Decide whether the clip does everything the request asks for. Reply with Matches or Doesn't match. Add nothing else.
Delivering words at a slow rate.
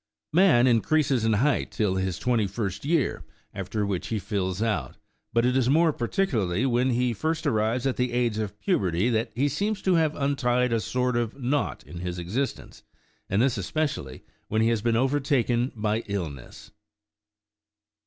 Doesn't match